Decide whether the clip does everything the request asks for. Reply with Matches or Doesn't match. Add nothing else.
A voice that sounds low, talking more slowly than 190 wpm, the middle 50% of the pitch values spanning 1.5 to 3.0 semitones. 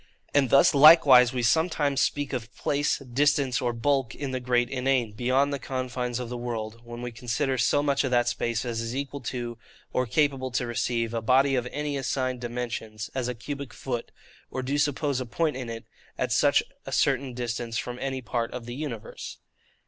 Doesn't match